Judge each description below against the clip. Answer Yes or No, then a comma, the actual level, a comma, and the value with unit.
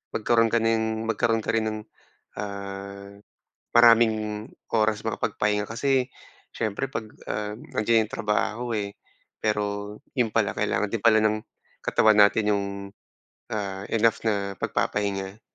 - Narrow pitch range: Yes, narrow, 1.7 semitones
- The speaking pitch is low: Yes, low, 110 Hz